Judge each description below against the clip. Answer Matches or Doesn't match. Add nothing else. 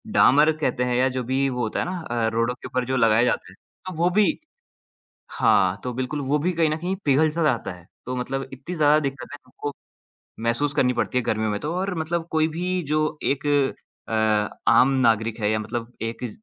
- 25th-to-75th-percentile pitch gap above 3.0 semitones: Matches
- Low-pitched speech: Matches